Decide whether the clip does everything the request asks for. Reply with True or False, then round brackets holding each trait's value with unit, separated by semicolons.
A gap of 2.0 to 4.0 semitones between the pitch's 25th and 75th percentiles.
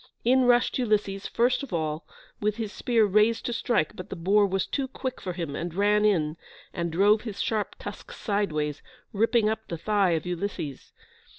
False (4.5 semitones)